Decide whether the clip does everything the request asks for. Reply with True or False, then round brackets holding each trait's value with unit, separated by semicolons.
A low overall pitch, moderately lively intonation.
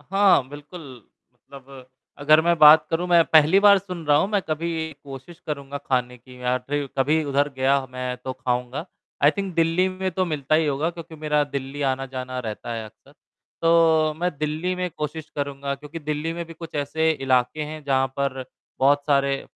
False (150 Hz; 3.4 semitones)